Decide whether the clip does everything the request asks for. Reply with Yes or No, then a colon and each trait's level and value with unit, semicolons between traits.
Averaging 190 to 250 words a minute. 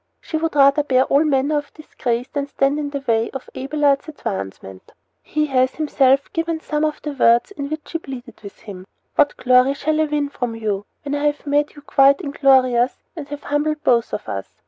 Yes: fast, 205 wpm